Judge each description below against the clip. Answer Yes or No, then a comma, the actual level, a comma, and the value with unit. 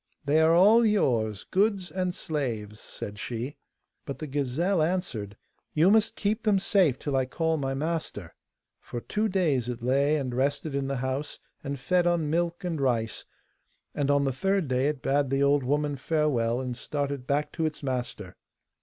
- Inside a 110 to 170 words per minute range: No, average, 180 wpm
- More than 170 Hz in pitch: No, medium, 145 Hz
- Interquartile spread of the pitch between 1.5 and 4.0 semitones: No, average, 4.9 semitones